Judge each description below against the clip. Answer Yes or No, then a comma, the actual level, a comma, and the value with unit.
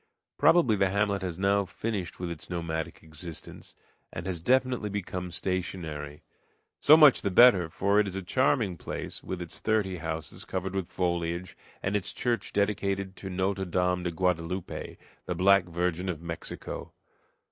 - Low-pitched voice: Yes, very low, 95 Hz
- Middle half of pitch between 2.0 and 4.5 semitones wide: Yes, narrow, 2.6 semitones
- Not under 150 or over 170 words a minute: Yes, average, 160 wpm